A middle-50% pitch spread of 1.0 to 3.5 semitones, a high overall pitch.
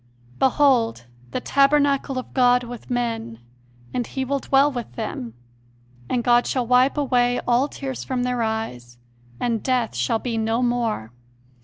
Yes: narrow, 2.5 semitones; high, 245 Hz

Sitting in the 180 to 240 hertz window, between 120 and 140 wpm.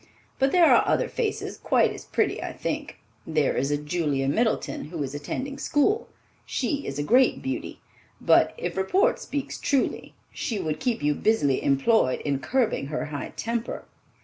No: high, 190 Hz; average, 170 wpm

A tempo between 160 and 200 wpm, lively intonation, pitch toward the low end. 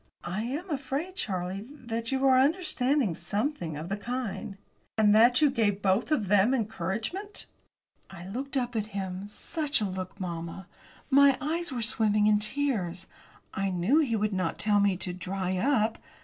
No: average, 170 wpm; wide, 5.8 semitones; high, 215 Hz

